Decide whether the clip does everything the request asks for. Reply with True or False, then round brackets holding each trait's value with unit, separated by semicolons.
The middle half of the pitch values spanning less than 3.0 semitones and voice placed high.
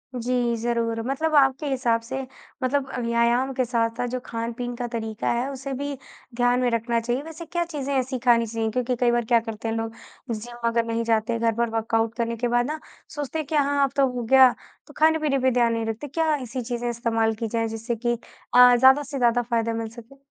True (2.5 semitones; 240 Hz)